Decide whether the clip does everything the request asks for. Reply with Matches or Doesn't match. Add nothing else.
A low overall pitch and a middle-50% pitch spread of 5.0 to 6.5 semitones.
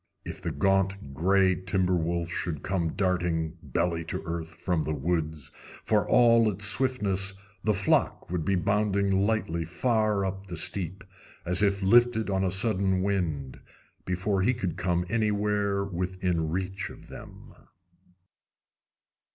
Doesn't match